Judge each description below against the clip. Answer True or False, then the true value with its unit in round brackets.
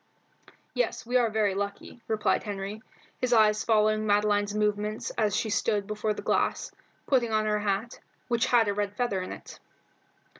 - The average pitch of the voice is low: False (215 Hz)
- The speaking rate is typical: True (165 wpm)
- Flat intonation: True (1.4 semitones)